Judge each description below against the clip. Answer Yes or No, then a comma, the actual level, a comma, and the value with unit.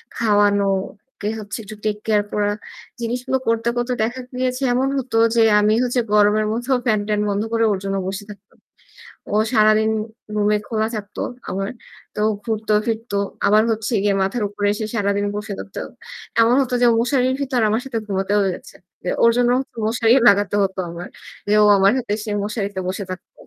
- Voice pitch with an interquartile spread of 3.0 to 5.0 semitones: No, narrow, 2.5 semitones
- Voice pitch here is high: Yes, high, 215 Hz